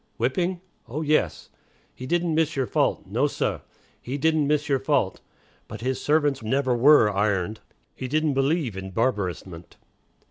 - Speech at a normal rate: Yes, average, 150 wpm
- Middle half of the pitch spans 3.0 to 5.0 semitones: No, wide, 5.5 semitones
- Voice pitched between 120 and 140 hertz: Yes, low, 135 Hz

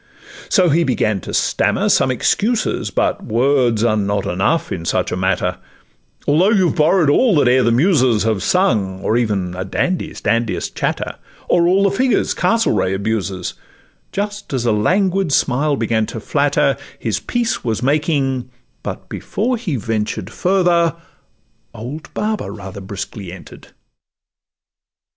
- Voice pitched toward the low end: Yes, low, 125 Hz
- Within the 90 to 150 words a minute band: Yes, average, 145 wpm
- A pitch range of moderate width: No, wide, 9.0 semitones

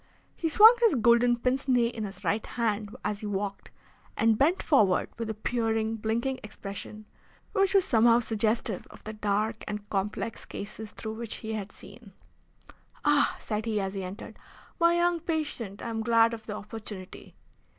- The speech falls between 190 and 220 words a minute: No, average, 170 wpm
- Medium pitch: No, high, 225 Hz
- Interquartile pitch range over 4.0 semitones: No, narrow, 2.6 semitones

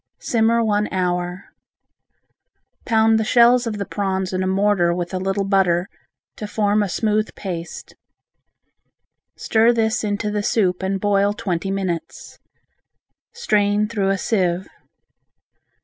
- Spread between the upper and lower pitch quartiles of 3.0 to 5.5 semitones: No, narrow, 2.5 semitones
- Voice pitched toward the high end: Yes, high, 200 Hz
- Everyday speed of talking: No, slow, 130 wpm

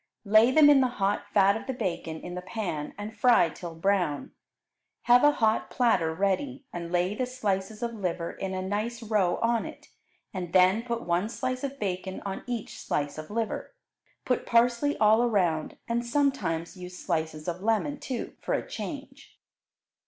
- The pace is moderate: Yes, average, 175 wpm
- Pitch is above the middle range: Yes, high, 210 Hz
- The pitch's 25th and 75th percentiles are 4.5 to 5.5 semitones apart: Yes, average, 5.1 semitones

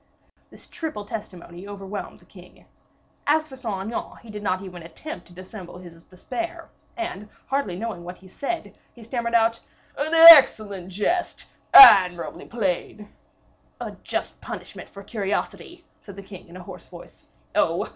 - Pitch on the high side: Yes, high, 205 Hz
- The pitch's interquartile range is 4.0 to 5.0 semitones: Yes, average, 4.5 semitones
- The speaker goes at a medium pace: Yes, average, 155 wpm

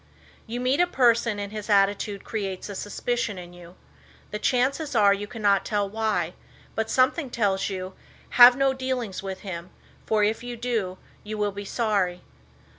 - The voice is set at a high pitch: Yes, high, 210 Hz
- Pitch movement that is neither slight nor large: Yes, average, 3.6 semitones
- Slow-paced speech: No, average, 170 wpm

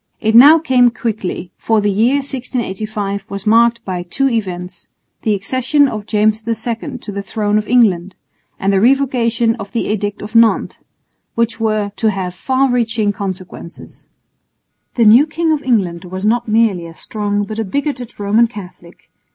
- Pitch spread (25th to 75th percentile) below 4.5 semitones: Yes, average, 3.2 semitones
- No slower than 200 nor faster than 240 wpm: No, average, 165 wpm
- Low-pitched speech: No, high, 220 Hz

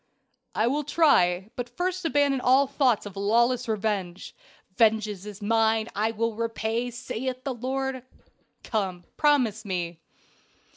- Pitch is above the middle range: Yes, high, 230 Hz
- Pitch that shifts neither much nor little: Yes, average, 3.7 semitones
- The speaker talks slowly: Yes, slow, 130 wpm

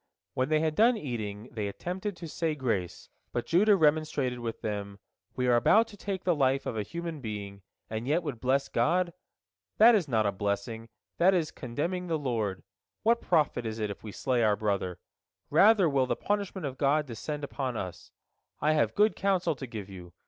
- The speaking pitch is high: No, low, 135 Hz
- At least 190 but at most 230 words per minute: Yes, average, 195 wpm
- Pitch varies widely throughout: Yes, wide, 7.6 semitones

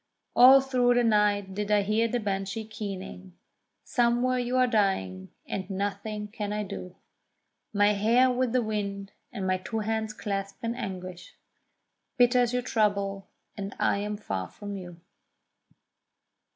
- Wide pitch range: No, average, 3.1 semitones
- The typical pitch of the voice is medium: No, high, 210 Hz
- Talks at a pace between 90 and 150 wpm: Yes, average, 145 wpm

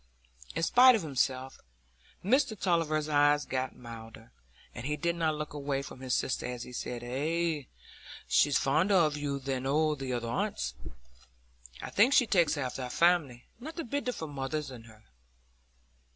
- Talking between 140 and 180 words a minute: Yes, average, 170 wpm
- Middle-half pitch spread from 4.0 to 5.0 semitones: Yes, average, 4.6 semitones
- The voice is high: No, medium, 145 Hz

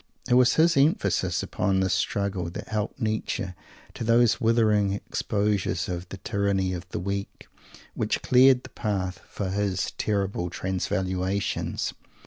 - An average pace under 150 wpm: Yes, slow, 135 wpm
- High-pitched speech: No, low, 100 Hz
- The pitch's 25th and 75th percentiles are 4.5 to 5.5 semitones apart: No, average, 2.8 semitones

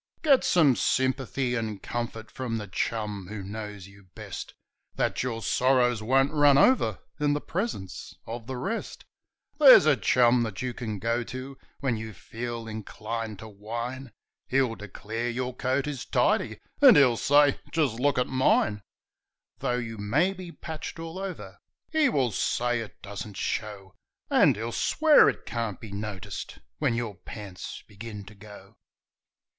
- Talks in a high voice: No, low, 120 Hz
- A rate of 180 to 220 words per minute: No, average, 160 wpm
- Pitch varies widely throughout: No, average, 3.9 semitones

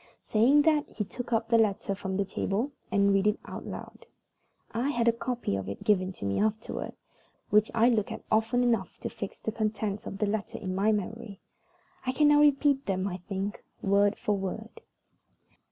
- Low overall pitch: No, high, 215 Hz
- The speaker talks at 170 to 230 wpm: Yes, average, 190 wpm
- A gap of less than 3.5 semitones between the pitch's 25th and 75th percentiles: Yes, average, 3.1 semitones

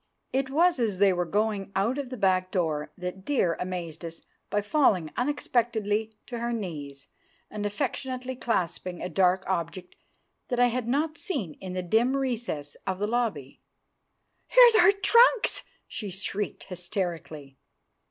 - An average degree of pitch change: No, wide, 5.7 semitones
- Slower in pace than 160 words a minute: Yes, average, 150 wpm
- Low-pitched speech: No, high, 205 Hz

